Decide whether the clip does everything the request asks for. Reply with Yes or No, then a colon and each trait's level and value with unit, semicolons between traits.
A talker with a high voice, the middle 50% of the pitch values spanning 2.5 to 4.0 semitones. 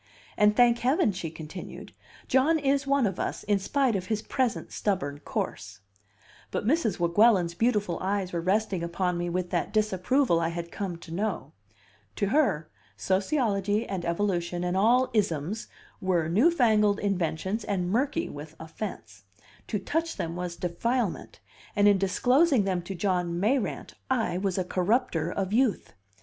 No: high, 195 Hz; average, 4.8 semitones